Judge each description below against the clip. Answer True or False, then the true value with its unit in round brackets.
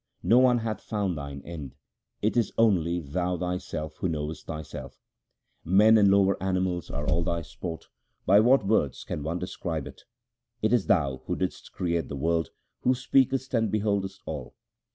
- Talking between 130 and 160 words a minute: False (175 wpm)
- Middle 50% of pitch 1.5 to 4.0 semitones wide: False (5.1 semitones)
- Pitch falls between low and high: False (90 Hz)